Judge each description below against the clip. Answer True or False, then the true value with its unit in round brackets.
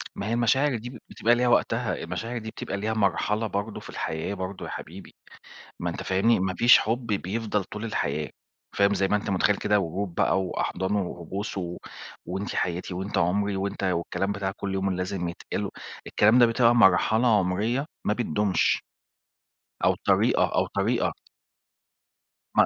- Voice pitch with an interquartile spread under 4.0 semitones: True (3.0 semitones)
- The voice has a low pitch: True (100 Hz)